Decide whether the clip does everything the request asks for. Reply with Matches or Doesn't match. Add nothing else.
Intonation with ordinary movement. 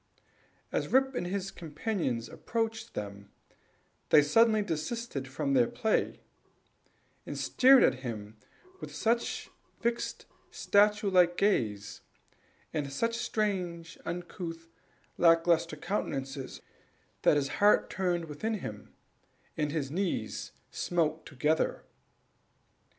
Doesn't match